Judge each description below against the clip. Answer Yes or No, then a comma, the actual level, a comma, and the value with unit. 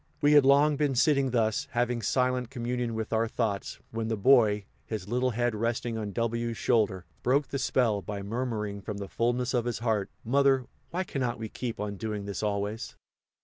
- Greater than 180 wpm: Yes, average, 190 wpm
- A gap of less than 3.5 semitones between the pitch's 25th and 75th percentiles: Yes, average, 3.0 semitones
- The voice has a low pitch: Yes, low, 115 Hz